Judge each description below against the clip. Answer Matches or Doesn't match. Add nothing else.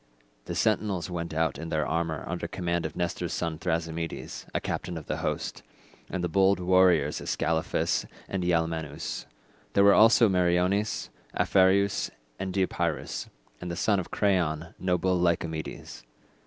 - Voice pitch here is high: Doesn't match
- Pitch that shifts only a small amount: Matches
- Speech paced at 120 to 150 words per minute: Matches